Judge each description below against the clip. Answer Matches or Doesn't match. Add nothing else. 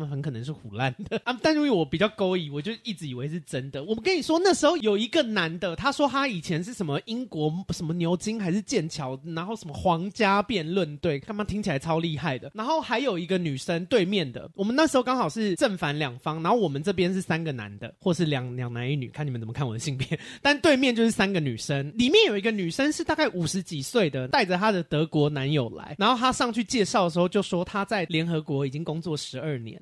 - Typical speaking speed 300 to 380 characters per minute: Matches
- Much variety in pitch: Matches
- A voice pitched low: Doesn't match